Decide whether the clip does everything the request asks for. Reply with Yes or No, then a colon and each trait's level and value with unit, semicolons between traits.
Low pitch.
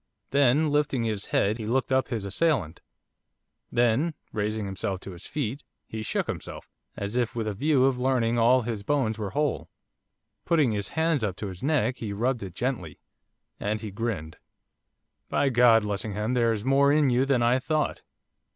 Yes: low, 120 Hz